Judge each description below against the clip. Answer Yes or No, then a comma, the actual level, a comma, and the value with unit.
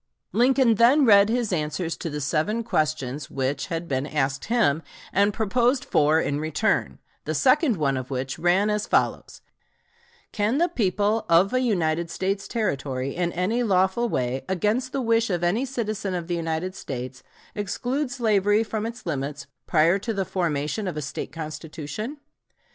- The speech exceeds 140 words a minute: Yes, average, 165 wpm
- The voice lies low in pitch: No, medium, 185 Hz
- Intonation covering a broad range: Yes, wide, 6.6 semitones